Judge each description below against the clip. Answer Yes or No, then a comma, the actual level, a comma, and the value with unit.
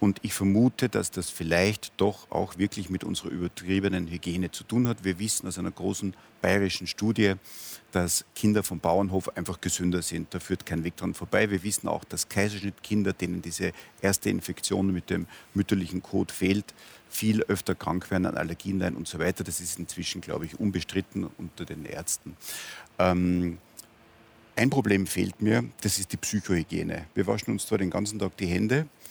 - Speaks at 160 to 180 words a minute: Yes, average, 175 wpm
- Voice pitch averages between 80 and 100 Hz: Yes, very low, 95 Hz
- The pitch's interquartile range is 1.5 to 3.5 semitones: Yes, average, 2.8 semitones